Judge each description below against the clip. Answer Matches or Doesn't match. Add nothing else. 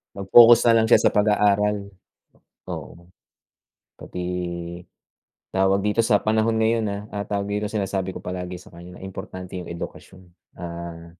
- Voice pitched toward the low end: Matches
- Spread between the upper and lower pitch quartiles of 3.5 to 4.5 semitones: Doesn't match